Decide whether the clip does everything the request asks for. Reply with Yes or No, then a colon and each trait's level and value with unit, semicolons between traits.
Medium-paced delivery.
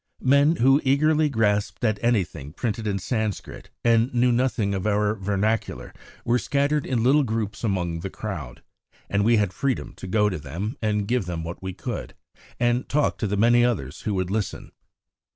Yes: average, 180 wpm